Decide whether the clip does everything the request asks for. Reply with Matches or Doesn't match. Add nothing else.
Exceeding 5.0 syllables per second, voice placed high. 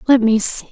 Matches